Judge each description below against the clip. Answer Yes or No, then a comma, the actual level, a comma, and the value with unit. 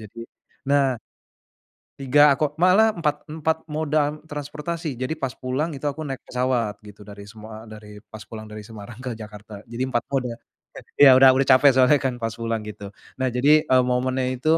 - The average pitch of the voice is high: No, low, 130 Hz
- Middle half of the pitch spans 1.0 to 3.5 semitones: No, average, 4.2 semitones